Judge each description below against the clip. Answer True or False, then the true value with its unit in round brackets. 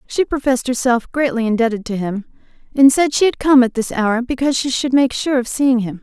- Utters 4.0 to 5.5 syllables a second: False (5.8 syllables/s)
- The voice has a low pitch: False (250 Hz)